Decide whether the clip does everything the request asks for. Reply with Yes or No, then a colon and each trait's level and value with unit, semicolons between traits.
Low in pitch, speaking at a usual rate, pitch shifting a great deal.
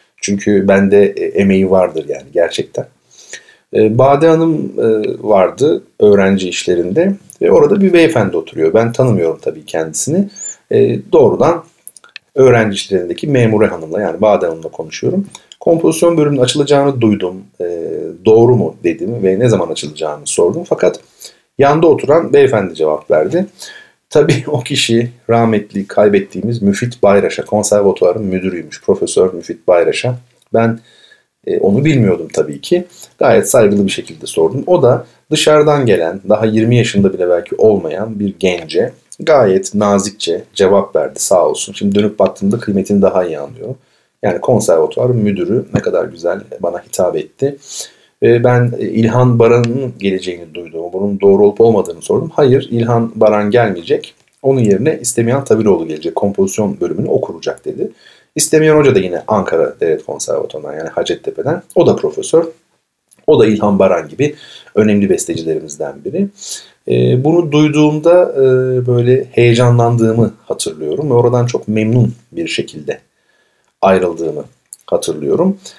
Yes: low, 120 Hz; average, 125 wpm; wide, 8.2 semitones